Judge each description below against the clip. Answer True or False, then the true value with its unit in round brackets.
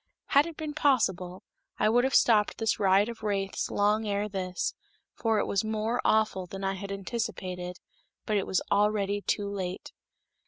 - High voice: True (205 Hz)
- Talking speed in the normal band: True (170 wpm)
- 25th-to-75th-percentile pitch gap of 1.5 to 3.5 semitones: True (2.4 semitones)